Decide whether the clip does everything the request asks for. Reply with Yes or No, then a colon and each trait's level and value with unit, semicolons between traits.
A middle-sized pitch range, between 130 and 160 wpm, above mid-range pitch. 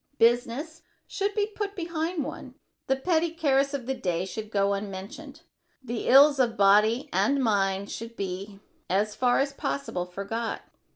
No: wide, 6.5 semitones; average, 155 wpm; high, 240 Hz